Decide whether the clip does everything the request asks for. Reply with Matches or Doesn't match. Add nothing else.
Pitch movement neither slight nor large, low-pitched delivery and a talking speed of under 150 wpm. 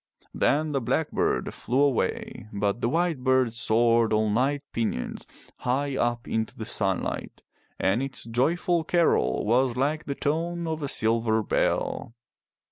Matches